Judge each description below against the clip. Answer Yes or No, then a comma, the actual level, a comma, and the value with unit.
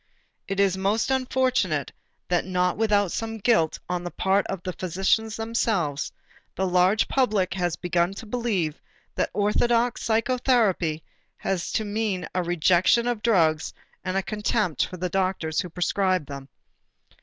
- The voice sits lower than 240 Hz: Yes, high, 190 Hz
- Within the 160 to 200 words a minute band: No, average, 145 wpm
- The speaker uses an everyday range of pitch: Yes, average, 3.9 semitones